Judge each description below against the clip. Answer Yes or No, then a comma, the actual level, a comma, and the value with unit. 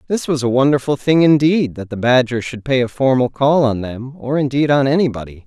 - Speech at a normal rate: No, fast, 220 wpm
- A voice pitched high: No, low, 130 Hz